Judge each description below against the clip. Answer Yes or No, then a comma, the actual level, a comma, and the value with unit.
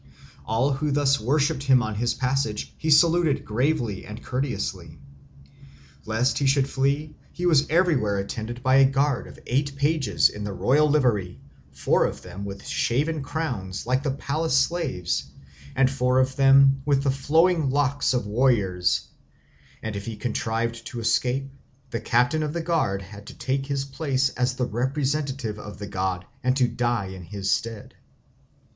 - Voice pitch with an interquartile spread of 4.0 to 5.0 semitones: Yes, average, 4.3 semitones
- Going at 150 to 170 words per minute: Yes, average, 165 wpm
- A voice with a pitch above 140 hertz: No, low, 130 Hz